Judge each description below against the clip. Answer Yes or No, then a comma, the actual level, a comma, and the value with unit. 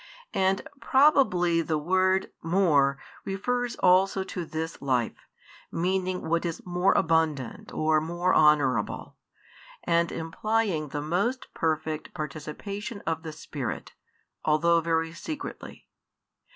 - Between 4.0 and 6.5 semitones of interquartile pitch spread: No, average, 3.4 semitones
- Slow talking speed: Yes, slow, 110 wpm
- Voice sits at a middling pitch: Yes, medium, 170 Hz